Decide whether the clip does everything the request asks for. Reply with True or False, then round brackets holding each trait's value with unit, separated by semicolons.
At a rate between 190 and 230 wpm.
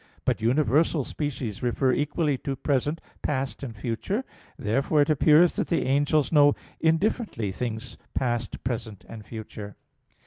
False (135 wpm)